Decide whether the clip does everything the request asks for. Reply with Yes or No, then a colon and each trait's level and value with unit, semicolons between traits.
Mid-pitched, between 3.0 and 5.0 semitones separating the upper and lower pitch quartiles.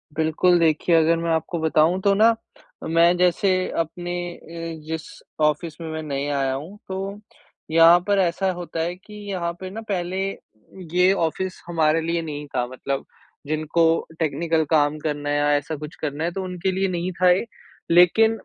No: medium, 165 Hz; narrow, 2.6 semitones